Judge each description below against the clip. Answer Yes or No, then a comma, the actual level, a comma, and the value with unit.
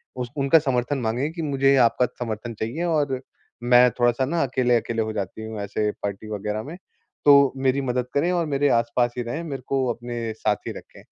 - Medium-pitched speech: No, low, 125 Hz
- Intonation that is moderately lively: Yes, average, 3.4 semitones